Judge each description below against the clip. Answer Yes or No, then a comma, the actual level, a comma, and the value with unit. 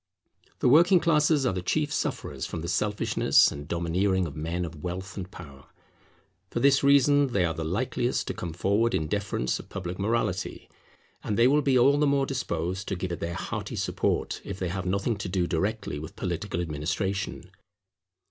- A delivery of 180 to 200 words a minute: Yes, average, 185 wpm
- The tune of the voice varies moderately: No, wide, 6.5 semitones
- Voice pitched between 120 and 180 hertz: No, very low, 95 Hz